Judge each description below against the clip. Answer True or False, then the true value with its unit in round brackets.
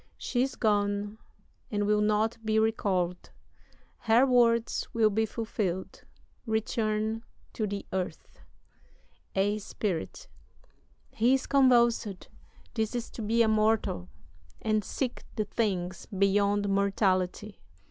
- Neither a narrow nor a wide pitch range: False (2.0 semitones)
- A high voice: True (215 Hz)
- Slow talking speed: True (110 wpm)